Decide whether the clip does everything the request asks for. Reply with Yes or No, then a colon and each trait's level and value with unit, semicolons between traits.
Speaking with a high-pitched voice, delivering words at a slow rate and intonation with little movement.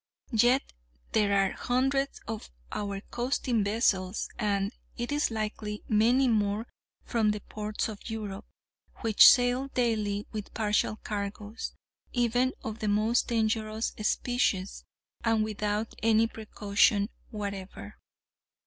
Yes: high, 215 Hz; slow, 115 wpm; narrow, 2.3 semitones